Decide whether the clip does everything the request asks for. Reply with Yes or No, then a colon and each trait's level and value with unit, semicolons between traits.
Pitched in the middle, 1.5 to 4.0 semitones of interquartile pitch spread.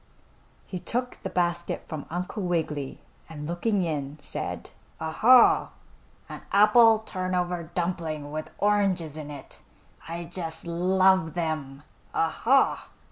Yes: medium, 175 Hz; average, 3.2 semitones